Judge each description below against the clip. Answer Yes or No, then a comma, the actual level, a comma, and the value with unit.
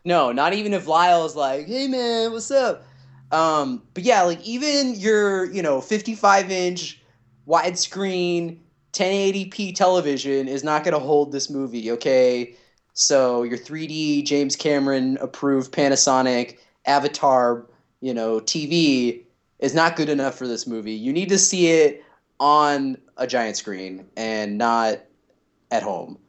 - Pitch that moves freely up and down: Yes, wide, 6.2 semitones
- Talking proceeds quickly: No, average, 140 wpm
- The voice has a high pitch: No, medium, 145 Hz